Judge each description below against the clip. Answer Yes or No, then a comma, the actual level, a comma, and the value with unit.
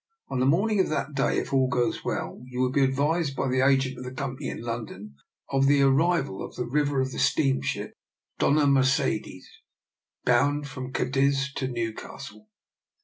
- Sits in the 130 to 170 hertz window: Yes, low, 135 Hz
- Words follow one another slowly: No, average, 185 wpm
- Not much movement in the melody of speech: Yes, narrow, 2.0 semitones